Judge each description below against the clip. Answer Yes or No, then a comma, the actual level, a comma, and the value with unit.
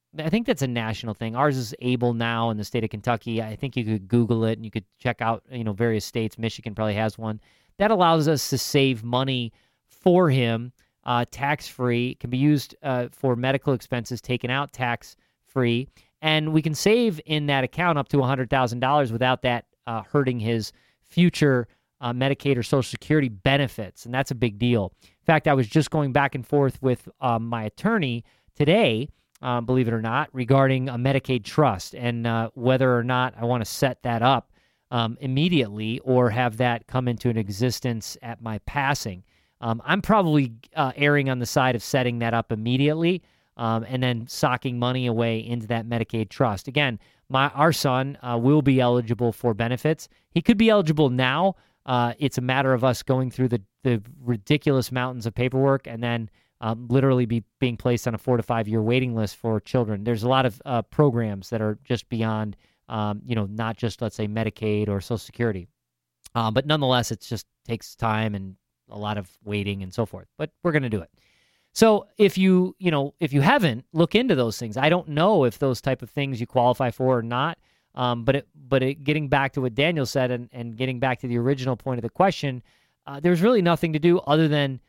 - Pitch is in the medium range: No, low, 125 Hz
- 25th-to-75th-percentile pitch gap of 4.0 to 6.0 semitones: No, average, 3.3 semitones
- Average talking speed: No, fast, 210 wpm